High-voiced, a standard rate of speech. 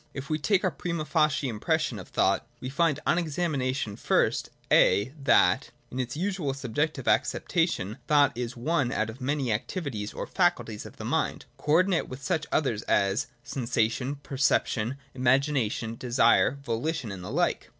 No: low, 135 Hz; average, 160 wpm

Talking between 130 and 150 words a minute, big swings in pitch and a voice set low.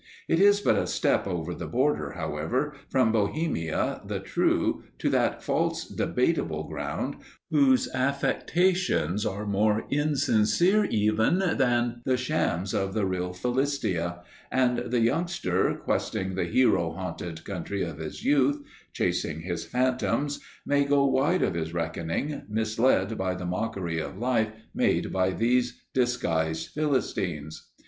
Yes: slow, 135 wpm; wide, 7.1 semitones; low, 110 Hz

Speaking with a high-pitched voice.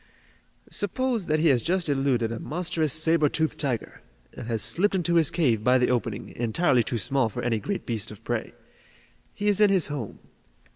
No: medium, 140 Hz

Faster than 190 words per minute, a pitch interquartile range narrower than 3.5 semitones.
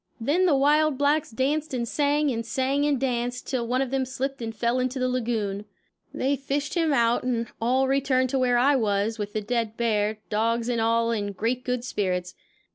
Yes: average, 200 wpm; average, 3.0 semitones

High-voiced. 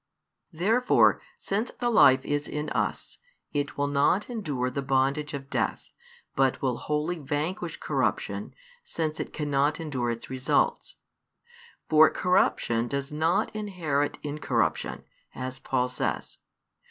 No: medium, 145 Hz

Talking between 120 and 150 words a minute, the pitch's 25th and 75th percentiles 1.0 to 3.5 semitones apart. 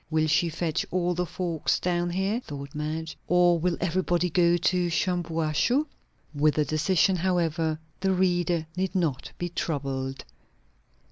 Yes: average, 140 wpm; narrow, 2.4 semitones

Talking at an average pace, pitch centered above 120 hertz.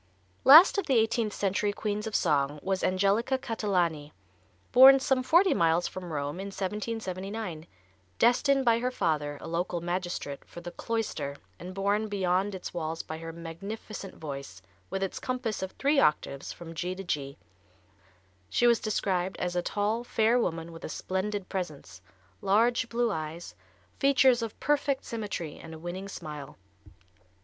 Yes: average, 155 wpm; high, 190 Hz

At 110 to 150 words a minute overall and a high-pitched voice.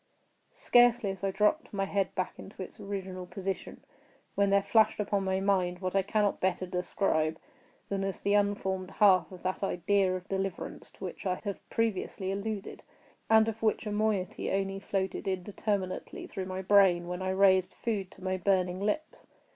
No: average, 175 wpm; high, 195 Hz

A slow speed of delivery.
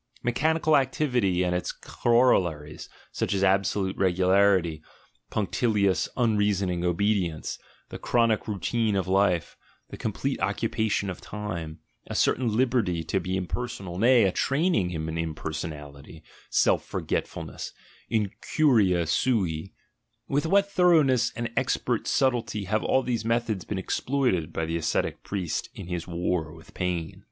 Yes: slow, 130 wpm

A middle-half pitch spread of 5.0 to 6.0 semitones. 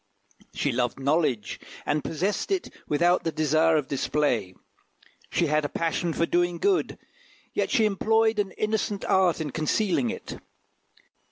Yes: wide, 5.4 semitones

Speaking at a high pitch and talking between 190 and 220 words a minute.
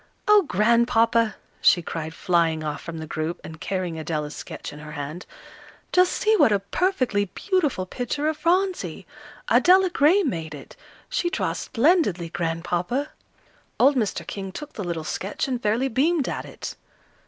No: high, 210 Hz; average, 155 wpm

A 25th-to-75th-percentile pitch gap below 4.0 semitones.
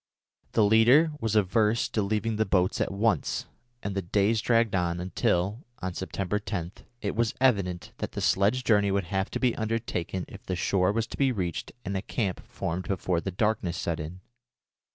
Yes: average, 3.4 semitones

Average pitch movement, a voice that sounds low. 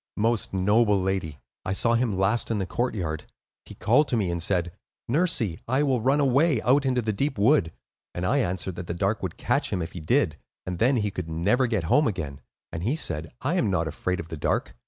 No: wide, 6.2 semitones; low, 105 Hz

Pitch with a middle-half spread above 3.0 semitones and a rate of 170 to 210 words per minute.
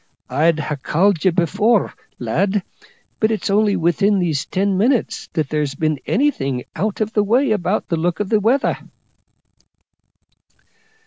No: average, 5.2 semitones; average, 145 wpm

